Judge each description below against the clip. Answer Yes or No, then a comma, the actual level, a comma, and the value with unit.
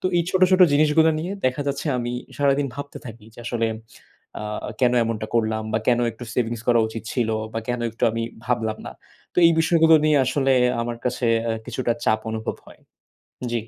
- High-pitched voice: No, low, 120 Hz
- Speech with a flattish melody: No, average, 3.9 semitones